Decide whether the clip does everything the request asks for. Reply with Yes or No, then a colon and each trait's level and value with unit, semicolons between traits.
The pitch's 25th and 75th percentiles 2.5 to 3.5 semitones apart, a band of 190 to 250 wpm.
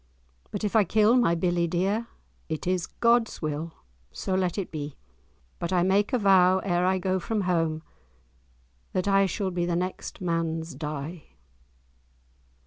No: average, 2.8 semitones; average, 155 wpm